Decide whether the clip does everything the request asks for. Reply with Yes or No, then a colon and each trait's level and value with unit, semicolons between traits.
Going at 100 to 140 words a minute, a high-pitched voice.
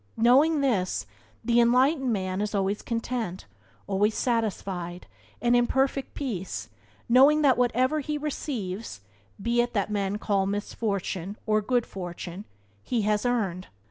Yes: slow, 135 wpm; high, 220 Hz